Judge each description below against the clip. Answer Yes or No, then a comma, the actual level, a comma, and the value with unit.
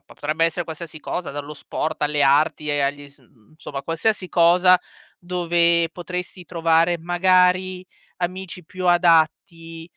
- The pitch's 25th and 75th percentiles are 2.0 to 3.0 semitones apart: Yes, narrow, 2.6 semitones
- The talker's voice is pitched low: No, medium, 170 Hz